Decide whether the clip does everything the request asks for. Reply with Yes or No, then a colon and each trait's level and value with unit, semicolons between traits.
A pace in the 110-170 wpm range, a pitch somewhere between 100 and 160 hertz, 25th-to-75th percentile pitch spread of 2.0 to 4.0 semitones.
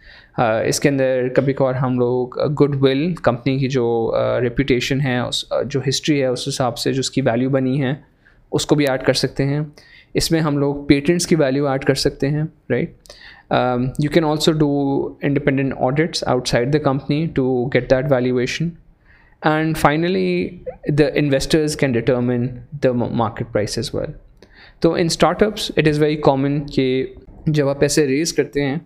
No: average, 180 wpm; medium, 140 Hz; average, 2.7 semitones